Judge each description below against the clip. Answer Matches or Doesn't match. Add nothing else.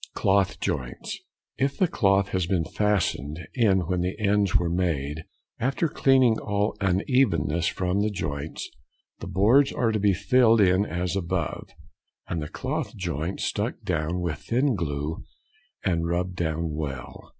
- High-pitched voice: Doesn't match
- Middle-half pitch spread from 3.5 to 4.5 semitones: Matches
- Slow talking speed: Doesn't match